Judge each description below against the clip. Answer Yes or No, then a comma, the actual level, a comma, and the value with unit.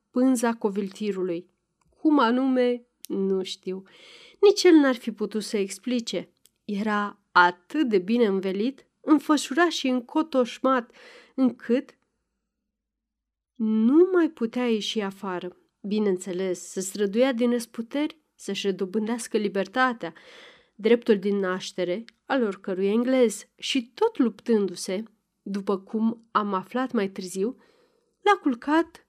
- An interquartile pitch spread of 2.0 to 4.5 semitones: No, average, 4.9 semitones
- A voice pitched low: No, high, 230 Hz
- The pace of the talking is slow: Yes, slow, 105 wpm